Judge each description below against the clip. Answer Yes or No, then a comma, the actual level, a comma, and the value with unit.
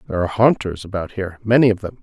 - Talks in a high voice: No, low, 100 Hz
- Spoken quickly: Yes, fast, 210 wpm